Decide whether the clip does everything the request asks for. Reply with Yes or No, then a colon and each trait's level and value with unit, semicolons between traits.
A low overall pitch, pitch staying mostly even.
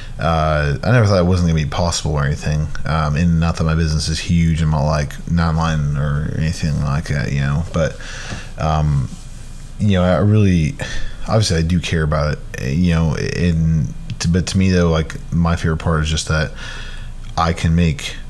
Yes: very low, 80 Hz; narrow, 2.0 semitones